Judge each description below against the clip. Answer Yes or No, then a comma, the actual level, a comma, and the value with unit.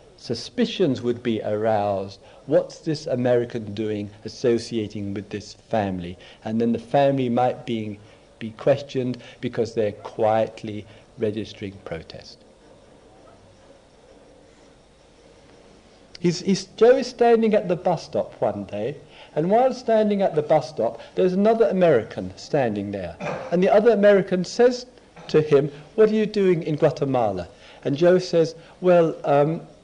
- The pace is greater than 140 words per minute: No, slow, 135 wpm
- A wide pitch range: Yes, wide, 8.7 semitones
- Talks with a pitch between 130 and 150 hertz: Yes, medium, 140 Hz